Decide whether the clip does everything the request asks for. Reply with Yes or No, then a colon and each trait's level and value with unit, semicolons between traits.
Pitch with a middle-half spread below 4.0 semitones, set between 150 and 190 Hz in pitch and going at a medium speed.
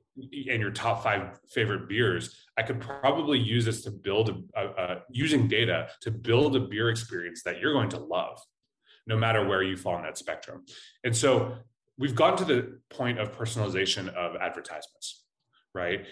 No: average, 3.2 semitones; low, 115 Hz; average, 180 wpm